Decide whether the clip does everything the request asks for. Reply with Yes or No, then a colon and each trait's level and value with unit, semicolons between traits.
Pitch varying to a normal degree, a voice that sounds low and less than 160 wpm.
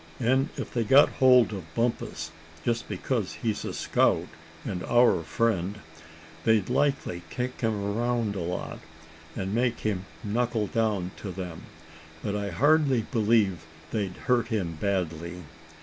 Yes: average, 4.2 semitones; low, 110 Hz; average, 140 wpm